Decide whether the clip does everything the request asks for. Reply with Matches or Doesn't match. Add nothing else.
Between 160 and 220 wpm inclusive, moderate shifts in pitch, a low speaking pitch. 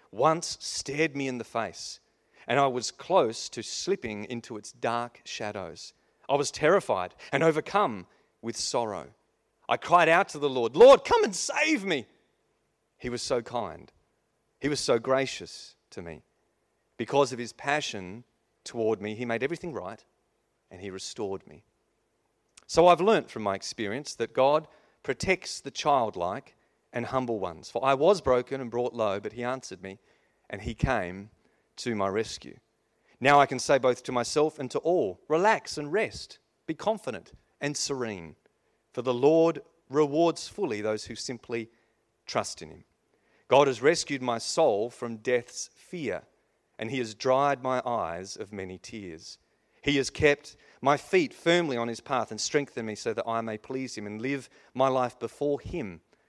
Matches